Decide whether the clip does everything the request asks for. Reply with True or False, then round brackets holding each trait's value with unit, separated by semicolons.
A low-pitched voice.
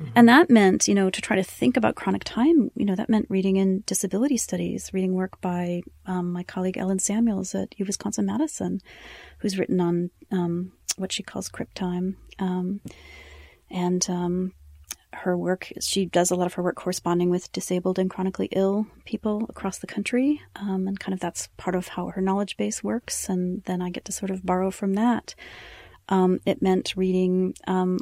False (190 Hz)